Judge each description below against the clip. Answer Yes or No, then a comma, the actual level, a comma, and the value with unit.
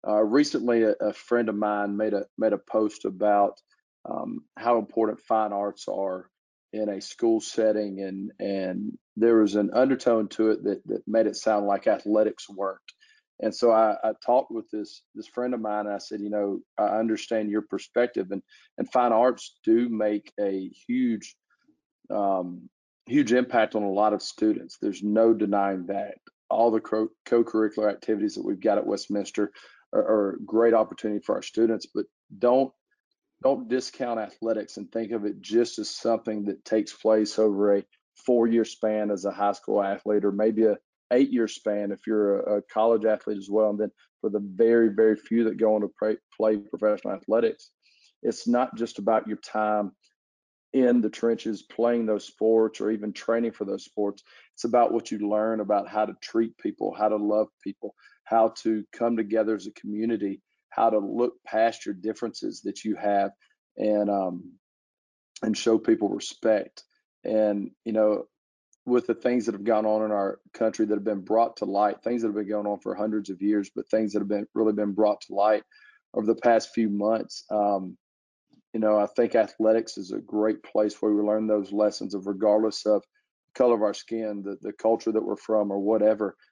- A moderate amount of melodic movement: No, narrow, 1.6 semitones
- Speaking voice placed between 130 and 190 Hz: No, low, 110 Hz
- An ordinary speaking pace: Yes, average, 190 wpm